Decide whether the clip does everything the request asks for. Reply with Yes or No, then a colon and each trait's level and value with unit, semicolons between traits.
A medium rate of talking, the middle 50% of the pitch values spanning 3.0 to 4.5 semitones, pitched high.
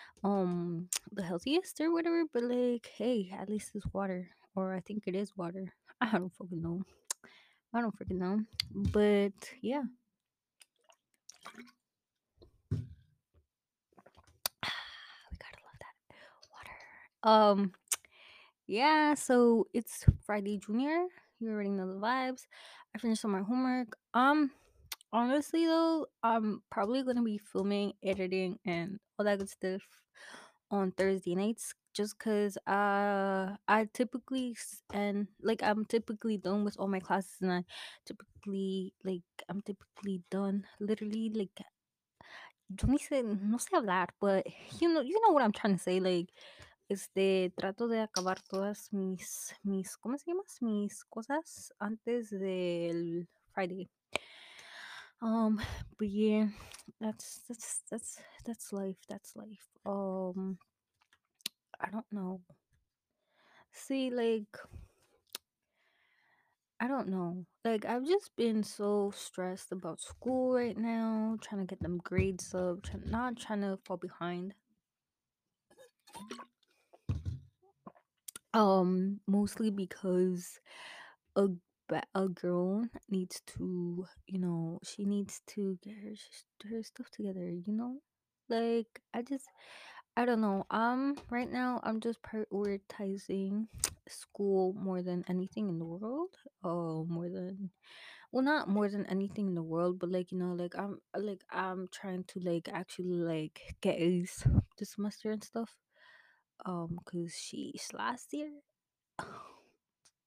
No: slow, 130 wpm; average, 3.6 semitones; high, 205 Hz